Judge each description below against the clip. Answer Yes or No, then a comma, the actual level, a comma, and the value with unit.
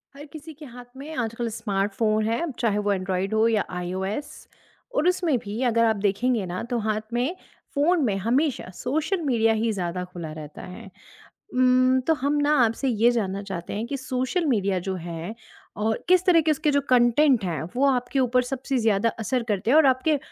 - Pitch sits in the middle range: No, high, 240 Hz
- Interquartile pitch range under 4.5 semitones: No, wide, 5.4 semitones